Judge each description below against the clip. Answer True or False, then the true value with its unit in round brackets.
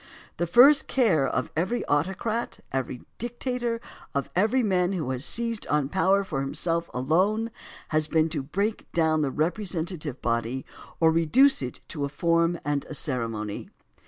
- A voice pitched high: False (165 Hz)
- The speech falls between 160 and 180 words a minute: True (165 wpm)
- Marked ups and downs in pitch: True (6.6 semitones)